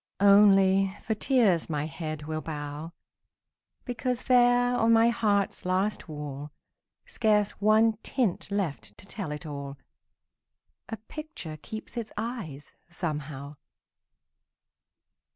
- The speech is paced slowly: Yes, slow, 110 wpm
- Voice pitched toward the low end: No, high, 195 Hz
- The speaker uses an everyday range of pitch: No, wide, 6.9 semitones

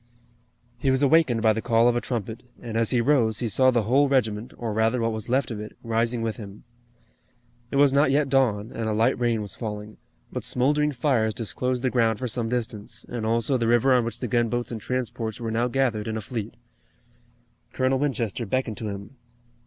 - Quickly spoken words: Yes, fast, 210 wpm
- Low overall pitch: Yes, low, 115 Hz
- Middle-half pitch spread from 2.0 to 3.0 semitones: Yes, narrow, 2.6 semitones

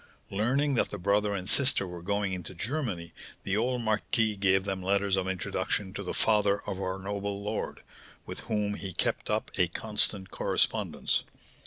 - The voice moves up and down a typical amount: No, narrow, 2.1 semitones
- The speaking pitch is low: Yes, low, 100 Hz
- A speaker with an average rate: Yes, average, 170 wpm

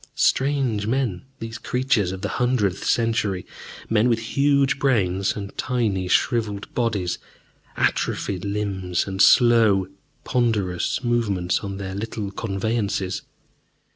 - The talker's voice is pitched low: Yes, low, 105 Hz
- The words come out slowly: Yes, slow, 110 wpm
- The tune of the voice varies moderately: Yes, average, 3.6 semitones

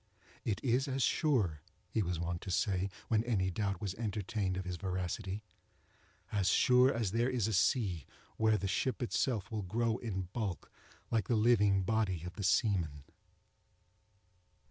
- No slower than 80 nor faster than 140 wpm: No, average, 160 wpm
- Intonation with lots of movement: No, average, 3.7 semitones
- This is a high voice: No, low, 105 Hz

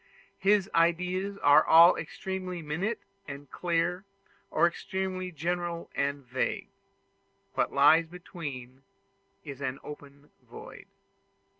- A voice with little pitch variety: No, average, 4.1 semitones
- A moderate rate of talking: No, slow, 110 wpm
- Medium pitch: Yes, medium, 170 Hz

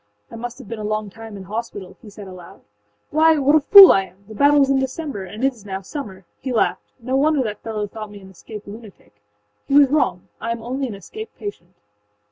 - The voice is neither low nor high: No, high, 225 Hz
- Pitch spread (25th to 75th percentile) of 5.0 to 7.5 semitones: Yes, average, 5.3 semitones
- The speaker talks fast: Yes, fast, 235 wpm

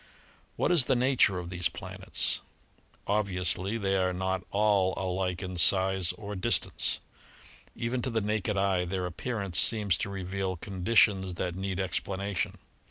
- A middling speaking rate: Yes, average, 145 wpm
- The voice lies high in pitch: No, very low, 95 Hz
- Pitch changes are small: Yes, narrow, 2.0 semitones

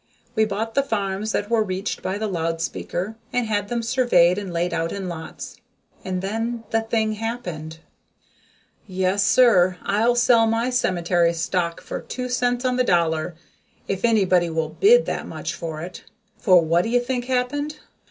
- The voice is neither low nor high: No, high, 205 Hz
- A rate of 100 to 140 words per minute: No, average, 170 wpm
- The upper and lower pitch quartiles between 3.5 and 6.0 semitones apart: Yes, average, 5.1 semitones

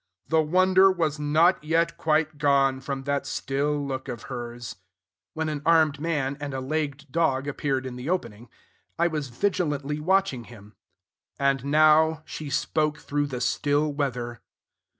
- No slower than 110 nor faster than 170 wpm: Yes, average, 150 wpm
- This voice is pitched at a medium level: Yes, medium, 145 Hz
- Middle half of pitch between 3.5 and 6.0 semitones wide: No, average, 2.9 semitones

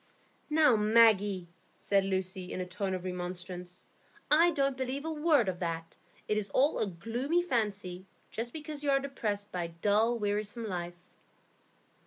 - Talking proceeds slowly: No, average, 160 wpm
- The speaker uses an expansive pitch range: Yes, wide, 6.3 semitones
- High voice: Yes, high, 210 Hz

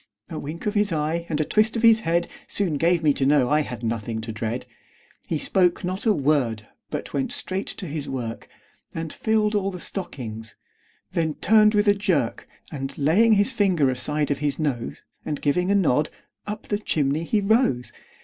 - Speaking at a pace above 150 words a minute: Yes, average, 195 wpm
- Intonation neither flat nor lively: No, wide, 6.5 semitones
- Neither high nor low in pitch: Yes, medium, 160 Hz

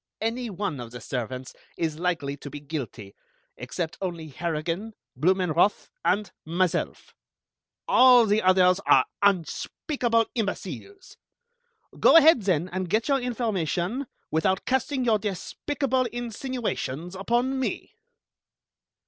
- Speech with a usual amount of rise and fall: No, wide, 6.8 semitones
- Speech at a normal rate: No, slow, 115 wpm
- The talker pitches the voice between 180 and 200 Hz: Yes, high, 190 Hz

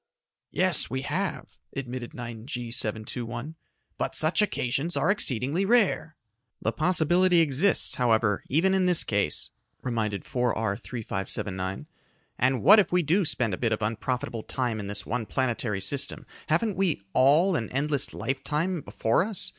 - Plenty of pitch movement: Yes, wide, 6.8 semitones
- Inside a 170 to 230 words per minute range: No, average, 145 wpm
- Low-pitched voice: Yes, low, 130 Hz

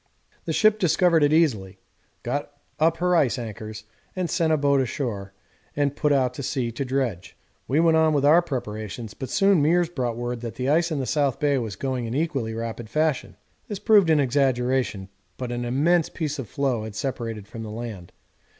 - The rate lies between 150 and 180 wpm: No, average, 195 wpm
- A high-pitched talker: No, low, 135 Hz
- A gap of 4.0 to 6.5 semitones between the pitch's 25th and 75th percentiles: Yes, average, 5.2 semitones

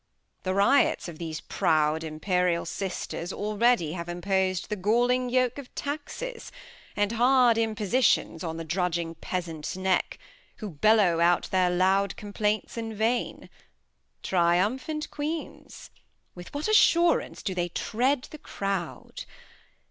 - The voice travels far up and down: Yes, wide, 5.7 semitones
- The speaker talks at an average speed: No, slow, 125 wpm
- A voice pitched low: No, high, 200 Hz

